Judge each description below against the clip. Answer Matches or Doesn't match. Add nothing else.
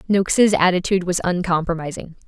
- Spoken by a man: Doesn't match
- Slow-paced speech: Matches